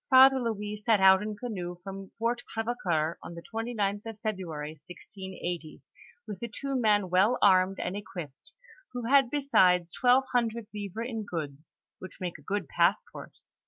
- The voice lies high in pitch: Yes, high, 205 Hz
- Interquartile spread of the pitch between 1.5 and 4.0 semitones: No, average, 4.4 semitones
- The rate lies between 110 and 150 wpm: No, average, 160 wpm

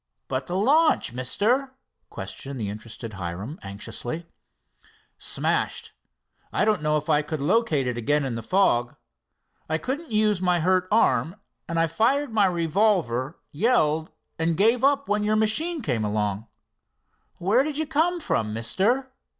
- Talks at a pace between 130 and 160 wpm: Yes, average, 150 wpm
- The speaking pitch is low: No, medium, 175 Hz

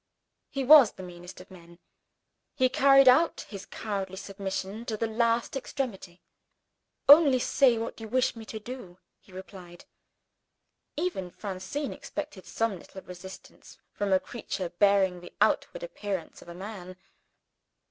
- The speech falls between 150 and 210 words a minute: No, average, 140 wpm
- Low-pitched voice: No, high, 205 Hz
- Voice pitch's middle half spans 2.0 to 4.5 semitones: No, average, 5.2 semitones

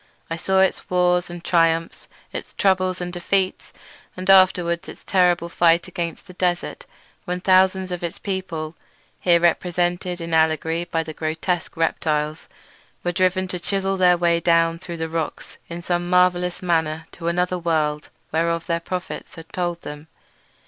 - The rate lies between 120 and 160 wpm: Yes, average, 150 wpm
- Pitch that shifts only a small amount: Yes, narrow, 1.6 semitones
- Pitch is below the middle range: No, medium, 175 Hz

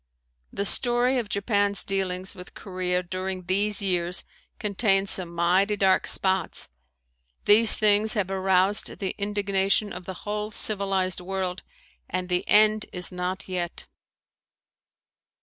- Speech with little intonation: Yes, narrow, 2.0 semitones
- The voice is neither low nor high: No, high, 195 Hz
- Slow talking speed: Yes, slow, 125 wpm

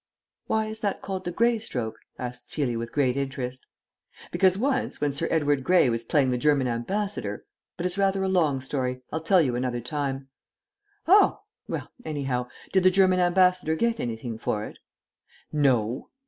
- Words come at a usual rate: Yes, average, 170 wpm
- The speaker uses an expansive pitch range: Yes, wide, 6.9 semitones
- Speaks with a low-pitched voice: No, medium, 145 Hz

